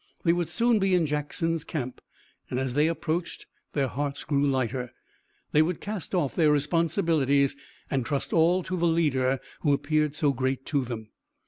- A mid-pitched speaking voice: Yes, medium, 150 Hz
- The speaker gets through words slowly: No, average, 175 wpm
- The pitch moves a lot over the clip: No, average, 3.6 semitones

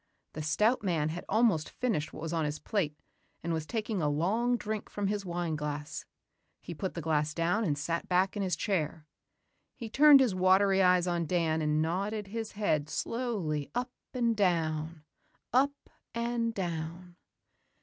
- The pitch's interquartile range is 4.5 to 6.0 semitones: Yes, wide, 5.4 semitones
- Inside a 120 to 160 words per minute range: No, average, 170 wpm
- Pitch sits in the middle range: Yes, medium, 180 Hz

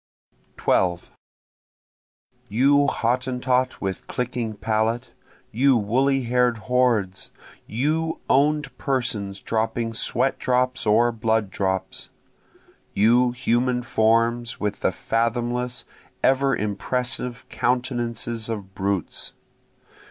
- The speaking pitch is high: No, low, 120 Hz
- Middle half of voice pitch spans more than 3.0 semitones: No, narrow, 2.5 semitones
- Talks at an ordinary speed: No, slow, 90 wpm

